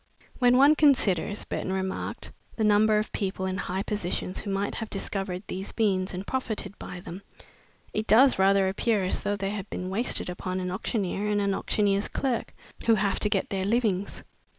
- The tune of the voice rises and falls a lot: No, narrow, 2.4 semitones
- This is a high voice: Yes, high, 200 Hz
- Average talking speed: Yes, average, 185 wpm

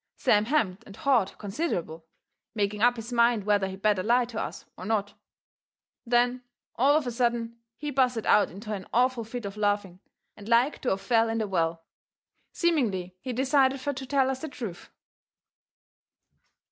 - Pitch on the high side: Yes, high, 230 Hz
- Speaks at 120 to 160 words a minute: No, average, 170 wpm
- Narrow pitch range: No, average, 4.0 semitones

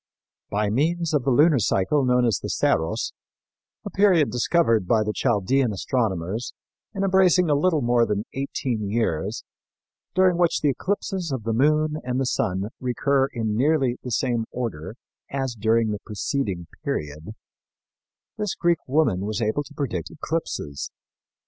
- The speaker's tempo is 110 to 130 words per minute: No, average, 150 wpm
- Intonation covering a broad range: Yes, wide, 6.1 semitones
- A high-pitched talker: No, low, 125 Hz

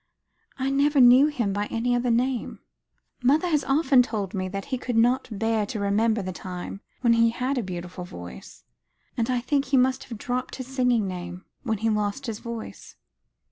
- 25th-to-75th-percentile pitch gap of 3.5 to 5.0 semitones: Yes, average, 4.1 semitones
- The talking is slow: No, average, 185 wpm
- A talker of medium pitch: No, high, 235 Hz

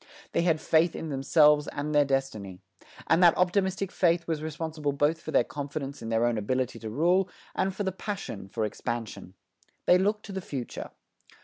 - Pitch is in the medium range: Yes, medium, 150 Hz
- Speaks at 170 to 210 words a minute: Yes, average, 185 wpm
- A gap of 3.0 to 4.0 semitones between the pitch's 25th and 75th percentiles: No, average, 5.2 semitones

